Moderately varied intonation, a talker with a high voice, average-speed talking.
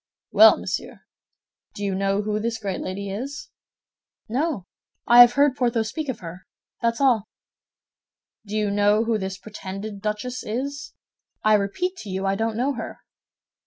Yes: average, 3.9 semitones; high, 215 Hz; average, 160 wpm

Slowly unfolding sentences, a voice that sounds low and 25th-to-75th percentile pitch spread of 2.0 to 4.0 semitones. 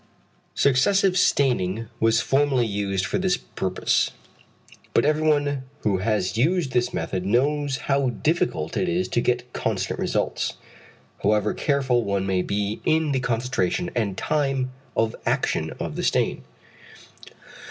No: slow, 130 wpm; low, 125 Hz; wide, 5.6 semitones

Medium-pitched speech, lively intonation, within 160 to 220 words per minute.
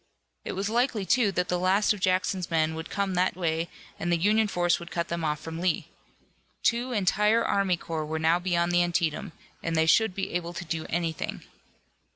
No: medium, 175 Hz; average, 3.1 semitones; average, 200 wpm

